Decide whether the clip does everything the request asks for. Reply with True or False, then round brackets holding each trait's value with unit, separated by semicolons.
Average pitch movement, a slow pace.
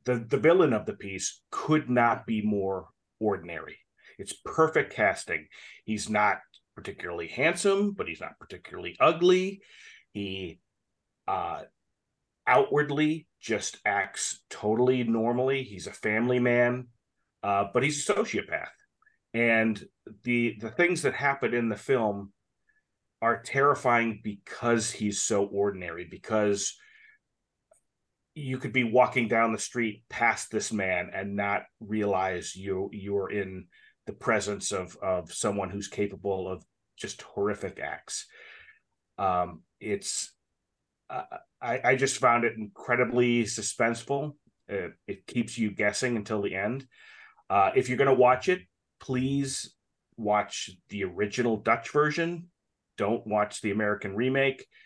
True (4.6 semitones; 130 wpm)